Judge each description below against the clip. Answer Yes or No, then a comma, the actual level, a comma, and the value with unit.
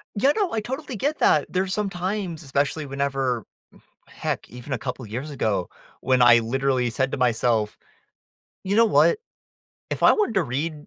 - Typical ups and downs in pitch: No, wide, 7.7 semitones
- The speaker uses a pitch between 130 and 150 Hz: Yes, medium, 140 Hz